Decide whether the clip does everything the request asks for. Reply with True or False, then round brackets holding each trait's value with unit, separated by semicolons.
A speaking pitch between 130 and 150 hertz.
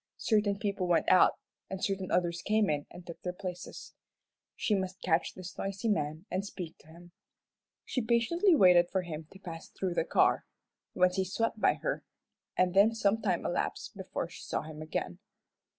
False (185 Hz)